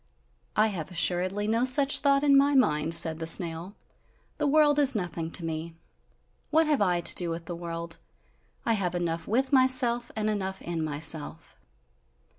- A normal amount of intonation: No, wide, 7.6 semitones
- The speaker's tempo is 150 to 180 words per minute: Yes, average, 170 wpm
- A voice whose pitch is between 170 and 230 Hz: Yes, medium, 185 Hz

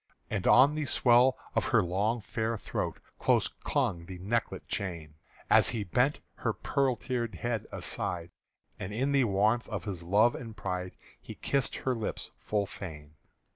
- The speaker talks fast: No, average, 165 wpm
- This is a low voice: Yes, low, 110 Hz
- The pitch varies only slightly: No, average, 4.7 semitones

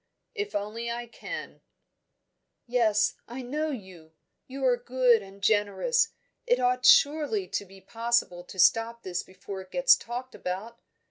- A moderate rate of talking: Yes, average, 145 wpm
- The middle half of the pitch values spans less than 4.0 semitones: No, average, 4.4 semitones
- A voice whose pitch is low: No, high, 235 Hz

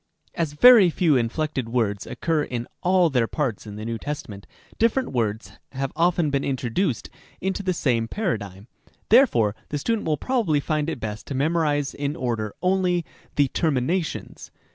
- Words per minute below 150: No, average, 160 wpm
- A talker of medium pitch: Yes, medium, 145 Hz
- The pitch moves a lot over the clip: Yes, wide, 6.8 semitones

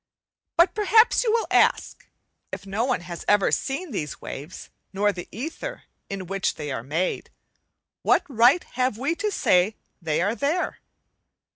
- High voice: Yes, high, 220 Hz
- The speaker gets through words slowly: No, average, 155 wpm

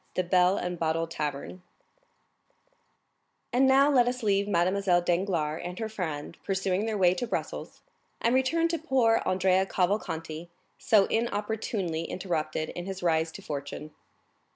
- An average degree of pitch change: Yes, average, 4.8 semitones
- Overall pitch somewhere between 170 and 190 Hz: Yes, medium, 185 Hz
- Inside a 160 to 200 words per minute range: No, average, 140 wpm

